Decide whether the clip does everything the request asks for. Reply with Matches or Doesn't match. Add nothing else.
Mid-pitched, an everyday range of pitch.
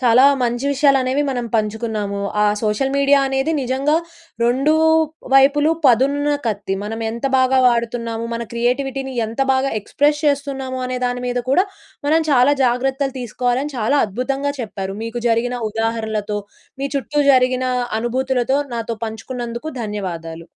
Doesn't match